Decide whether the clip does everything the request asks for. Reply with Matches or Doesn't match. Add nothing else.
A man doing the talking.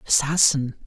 Matches